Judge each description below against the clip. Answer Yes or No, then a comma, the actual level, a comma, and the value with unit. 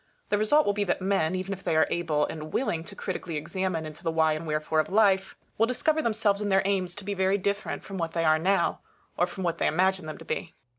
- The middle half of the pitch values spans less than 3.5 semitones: No, average, 3.8 semitones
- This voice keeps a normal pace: No, fast, 255 wpm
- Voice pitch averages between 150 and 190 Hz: Yes, medium, 185 Hz